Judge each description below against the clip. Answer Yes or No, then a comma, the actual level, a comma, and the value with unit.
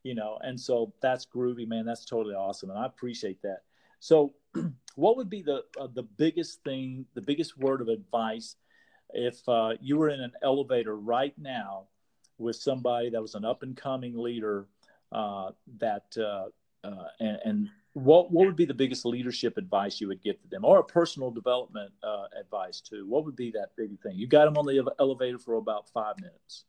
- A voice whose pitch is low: Yes, low, 125 Hz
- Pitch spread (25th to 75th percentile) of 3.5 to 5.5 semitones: Yes, average, 3.8 semitones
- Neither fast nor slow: Yes, average, 195 wpm